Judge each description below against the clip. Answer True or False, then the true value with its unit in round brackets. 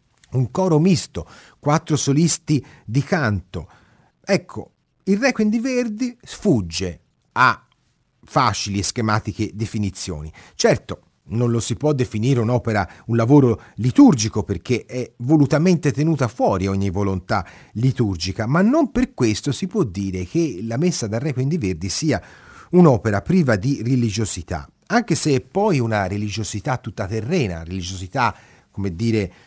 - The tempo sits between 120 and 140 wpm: True (135 wpm)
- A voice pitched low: True (120 Hz)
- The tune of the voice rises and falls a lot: True (7.4 semitones)